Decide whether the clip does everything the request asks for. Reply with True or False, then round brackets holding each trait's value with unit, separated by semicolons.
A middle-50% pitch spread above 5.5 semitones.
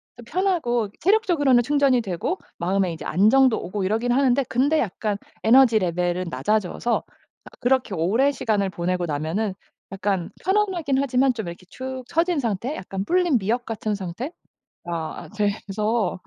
True (5.9 semitones)